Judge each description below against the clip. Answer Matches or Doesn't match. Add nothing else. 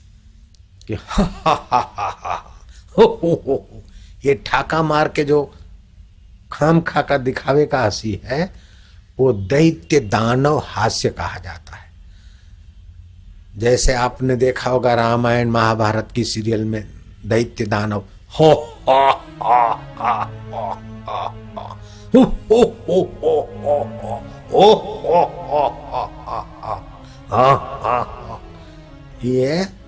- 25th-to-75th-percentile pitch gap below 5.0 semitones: Doesn't match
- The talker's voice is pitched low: Matches